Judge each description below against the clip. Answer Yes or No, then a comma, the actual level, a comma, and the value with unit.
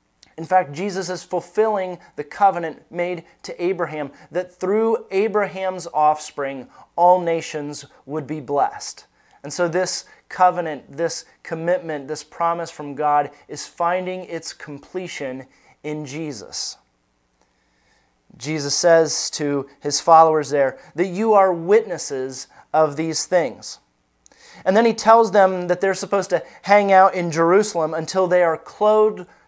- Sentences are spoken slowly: Yes, slow, 130 wpm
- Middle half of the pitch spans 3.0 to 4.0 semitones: Yes, average, 3.5 semitones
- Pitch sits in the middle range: Yes, medium, 170 Hz